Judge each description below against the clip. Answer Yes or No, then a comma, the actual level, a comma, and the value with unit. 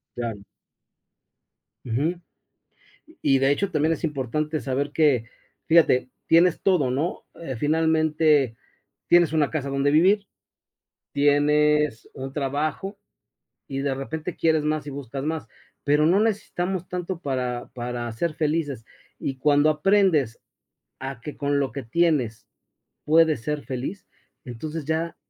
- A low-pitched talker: No, medium, 150 Hz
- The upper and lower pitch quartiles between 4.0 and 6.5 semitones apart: No, average, 3.2 semitones